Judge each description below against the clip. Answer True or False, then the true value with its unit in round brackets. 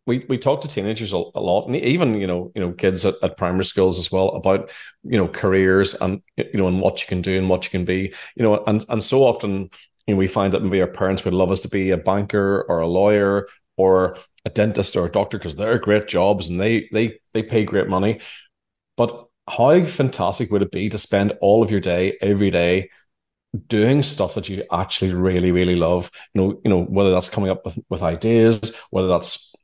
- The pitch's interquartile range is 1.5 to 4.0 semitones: True (2.6 semitones)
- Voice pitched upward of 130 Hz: False (95 Hz)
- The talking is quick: True (230 wpm)